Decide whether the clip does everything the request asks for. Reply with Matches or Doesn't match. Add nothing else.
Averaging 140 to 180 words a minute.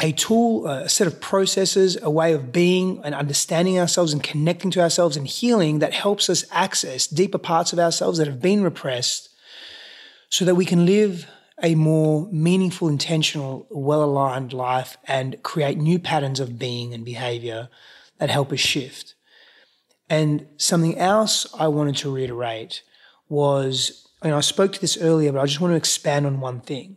Matches